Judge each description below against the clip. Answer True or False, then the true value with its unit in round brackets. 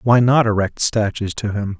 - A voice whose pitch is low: True (105 Hz)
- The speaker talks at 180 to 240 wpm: True (200 wpm)